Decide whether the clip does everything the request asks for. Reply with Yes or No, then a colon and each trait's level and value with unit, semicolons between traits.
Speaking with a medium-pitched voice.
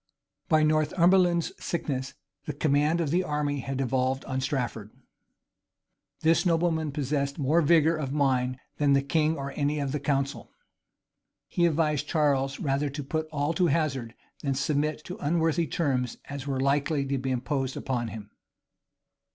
Yes: medium, 145 Hz